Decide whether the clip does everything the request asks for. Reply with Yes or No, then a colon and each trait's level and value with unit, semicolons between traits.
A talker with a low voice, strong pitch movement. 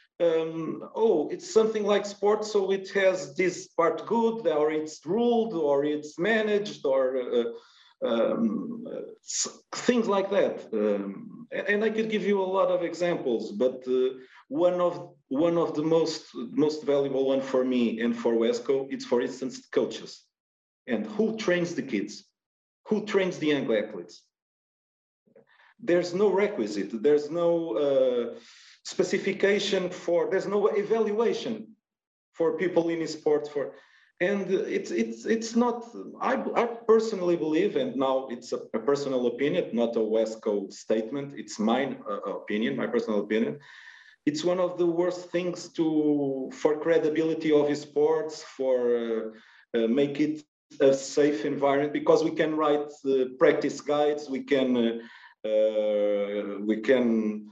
No: medium, 165 Hz; wide, 7.2 semitones